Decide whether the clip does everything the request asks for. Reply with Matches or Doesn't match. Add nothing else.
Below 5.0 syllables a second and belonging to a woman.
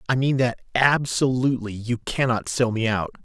Doesn't match